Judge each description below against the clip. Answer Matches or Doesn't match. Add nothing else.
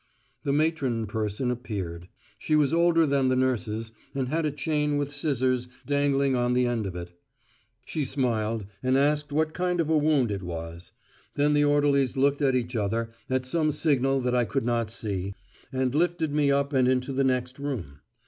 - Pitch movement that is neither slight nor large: Matches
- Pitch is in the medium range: Doesn't match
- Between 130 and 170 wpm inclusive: Doesn't match